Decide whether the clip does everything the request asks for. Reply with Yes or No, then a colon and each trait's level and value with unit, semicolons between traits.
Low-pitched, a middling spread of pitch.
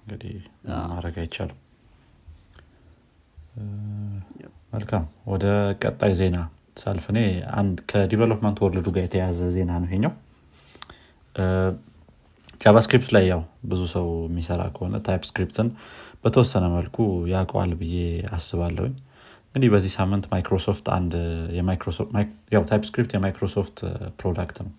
Yes: very low, 95 Hz; average, 3.2 semitones